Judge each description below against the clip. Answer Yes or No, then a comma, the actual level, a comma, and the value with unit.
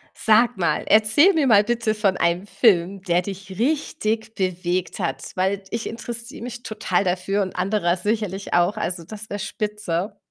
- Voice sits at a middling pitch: No, high, 205 Hz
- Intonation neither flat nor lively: Yes, average, 3.2 semitones